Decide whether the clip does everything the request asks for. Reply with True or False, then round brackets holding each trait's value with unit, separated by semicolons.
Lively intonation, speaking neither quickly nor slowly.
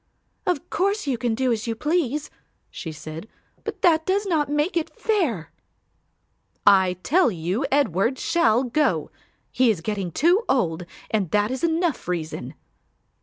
True (8.9 semitones; 150 wpm)